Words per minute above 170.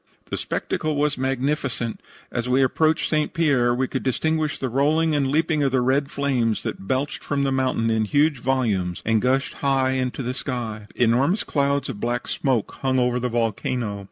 Yes: average, 185 wpm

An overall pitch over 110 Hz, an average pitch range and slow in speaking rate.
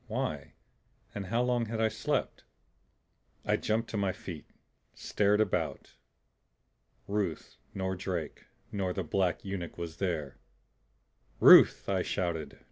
No: very low, 95 Hz; average, 3.7 semitones; slow, 125 wpm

